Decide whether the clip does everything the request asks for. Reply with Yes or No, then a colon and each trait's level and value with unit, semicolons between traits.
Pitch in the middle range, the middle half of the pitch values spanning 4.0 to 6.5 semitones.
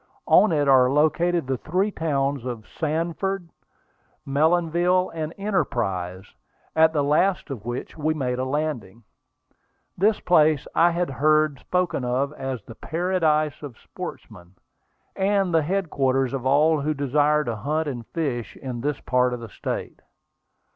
Yes: medium, 150 Hz; average, 4.3 semitones